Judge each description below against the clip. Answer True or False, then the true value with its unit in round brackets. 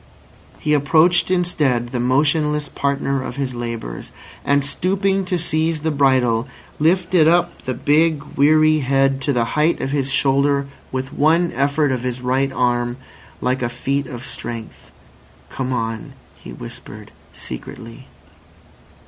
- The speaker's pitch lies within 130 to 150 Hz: True (140 Hz)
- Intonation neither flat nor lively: True (3.7 semitones)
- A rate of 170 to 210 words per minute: False (140 wpm)